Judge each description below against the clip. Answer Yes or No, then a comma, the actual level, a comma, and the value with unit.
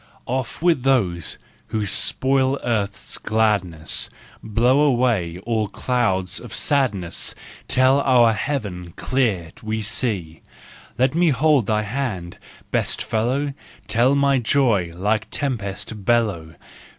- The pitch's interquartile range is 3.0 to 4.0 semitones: No, average, 4.9 semitones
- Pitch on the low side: Yes, low, 115 Hz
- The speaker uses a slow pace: Yes, slow, 115 wpm